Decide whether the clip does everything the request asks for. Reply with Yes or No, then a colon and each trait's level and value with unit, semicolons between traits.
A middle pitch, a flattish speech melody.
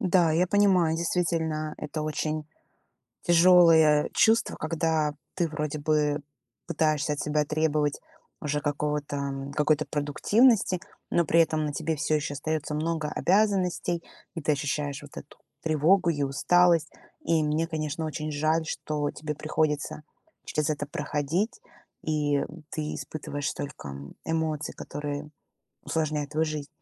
Yes: medium, 155 Hz; narrow, 1.9 semitones